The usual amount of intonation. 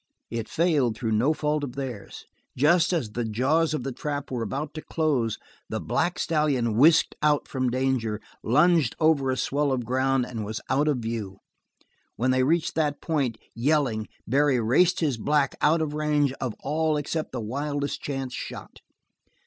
Yes: average, 3.8 semitones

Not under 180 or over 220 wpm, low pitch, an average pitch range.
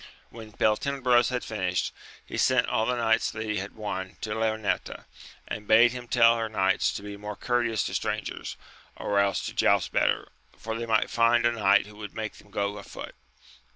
No: average, 190 wpm; low, 110 Hz; narrow, 2.2 semitones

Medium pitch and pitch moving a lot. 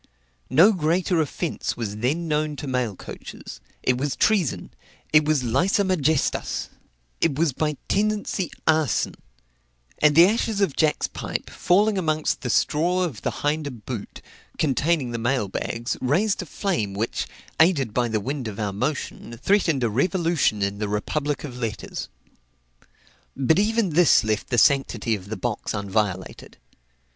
Yes: medium, 145 Hz; wide, 6.4 semitones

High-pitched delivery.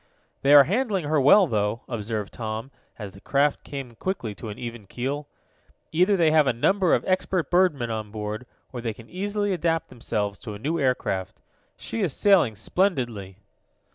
No: low, 130 Hz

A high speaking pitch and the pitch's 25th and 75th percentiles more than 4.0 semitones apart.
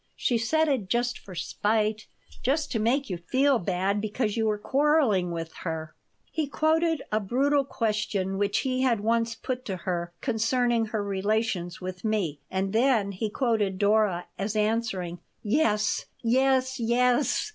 Yes: high, 220 Hz; average, 4.5 semitones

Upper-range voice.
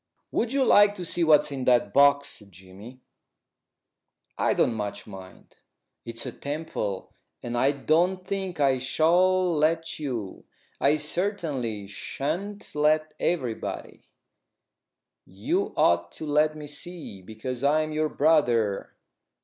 No: medium, 145 Hz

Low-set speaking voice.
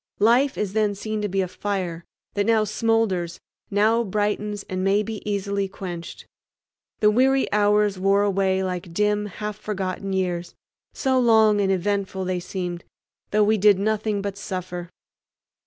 No: high, 205 Hz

